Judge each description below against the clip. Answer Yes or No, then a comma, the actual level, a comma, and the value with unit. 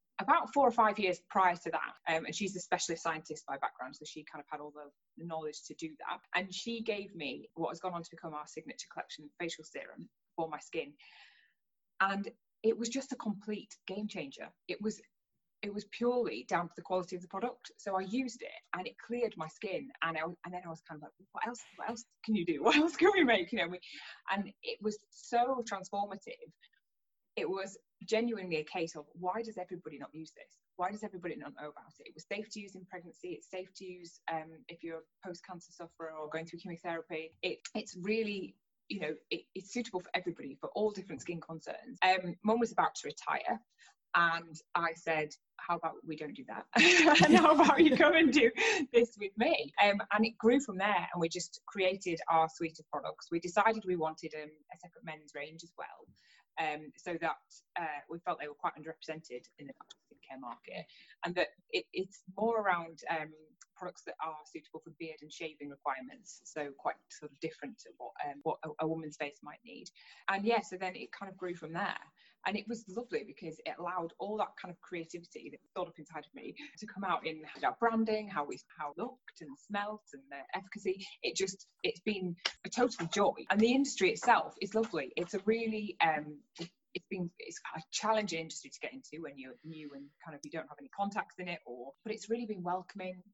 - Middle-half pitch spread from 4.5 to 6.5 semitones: Yes, average, 4.9 semitones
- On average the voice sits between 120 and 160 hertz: No, medium, 180 Hz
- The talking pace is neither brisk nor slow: No, fast, 220 wpm